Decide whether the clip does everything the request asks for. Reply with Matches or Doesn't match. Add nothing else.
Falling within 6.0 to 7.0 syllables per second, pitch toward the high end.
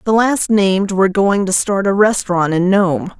Doesn't match